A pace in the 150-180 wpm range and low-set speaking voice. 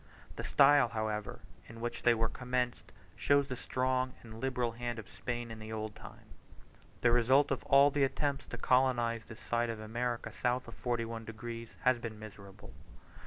Yes: average, 175 wpm; low, 120 Hz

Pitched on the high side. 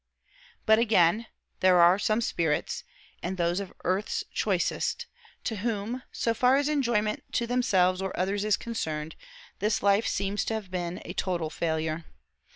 Yes: high, 200 Hz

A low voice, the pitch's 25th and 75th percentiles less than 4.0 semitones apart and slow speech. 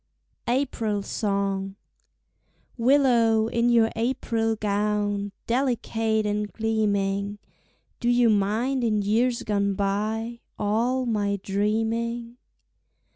No: high, 220 Hz; narrow, 2.5 semitones; slow, 90 wpm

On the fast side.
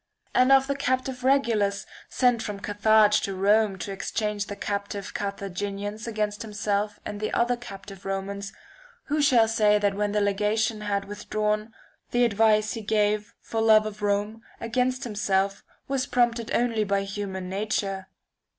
No: average, 155 wpm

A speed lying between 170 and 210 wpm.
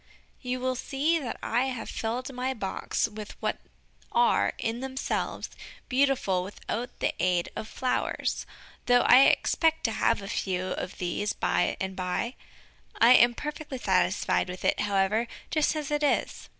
No: average, 155 wpm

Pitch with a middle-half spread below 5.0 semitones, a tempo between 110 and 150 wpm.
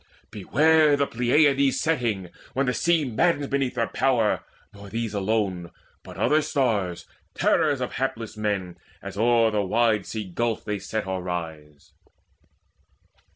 No: average, 5.3 semitones; average, 140 wpm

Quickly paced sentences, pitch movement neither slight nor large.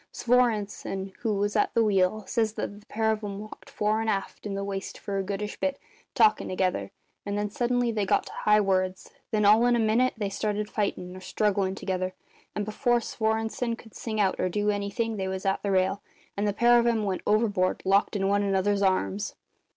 No: fast, 215 wpm; narrow, 2.1 semitones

